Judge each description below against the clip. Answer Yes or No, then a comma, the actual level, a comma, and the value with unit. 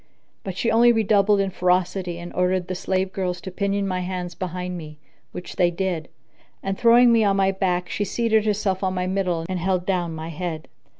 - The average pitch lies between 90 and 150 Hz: No, medium, 185 Hz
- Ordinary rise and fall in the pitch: No, narrow, 1.7 semitones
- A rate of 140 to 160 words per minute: No, average, 200 wpm